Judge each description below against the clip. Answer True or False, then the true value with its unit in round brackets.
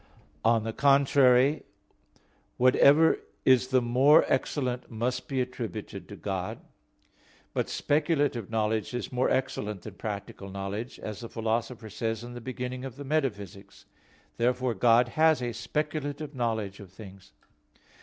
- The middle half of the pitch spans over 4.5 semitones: False (3.3 semitones)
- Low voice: True (120 Hz)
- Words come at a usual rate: False (130 wpm)